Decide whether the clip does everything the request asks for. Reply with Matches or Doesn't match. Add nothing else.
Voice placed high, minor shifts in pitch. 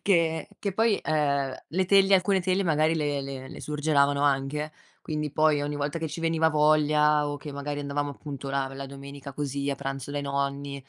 Doesn't match